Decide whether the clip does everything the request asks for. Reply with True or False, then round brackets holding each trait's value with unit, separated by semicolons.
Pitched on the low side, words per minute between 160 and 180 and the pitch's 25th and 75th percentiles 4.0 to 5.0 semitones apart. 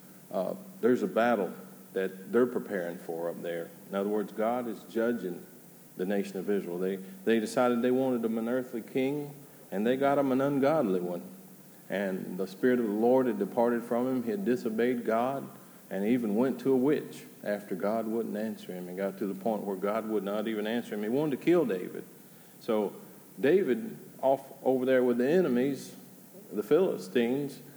False (115 Hz; 190 wpm; 4.3 semitones)